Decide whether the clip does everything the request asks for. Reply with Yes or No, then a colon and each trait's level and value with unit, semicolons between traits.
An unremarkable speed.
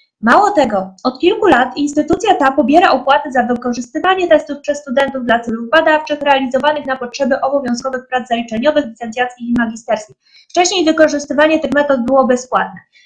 Yes: average, 145 wpm